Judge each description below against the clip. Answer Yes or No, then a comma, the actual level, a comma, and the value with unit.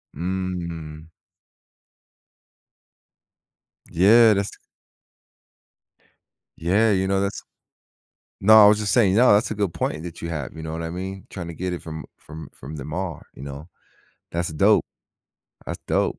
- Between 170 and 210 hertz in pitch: No, very low, 90 Hz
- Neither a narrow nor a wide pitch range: Yes, average, 3.8 semitones